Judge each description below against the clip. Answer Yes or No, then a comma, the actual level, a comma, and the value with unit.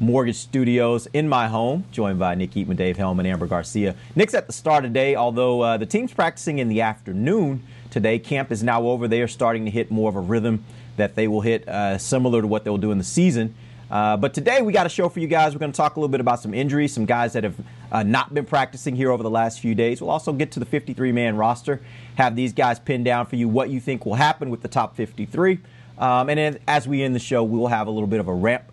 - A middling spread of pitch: Yes, average, 3.5 semitones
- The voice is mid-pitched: No, low, 120 Hz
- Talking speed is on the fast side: Yes, fast, 265 wpm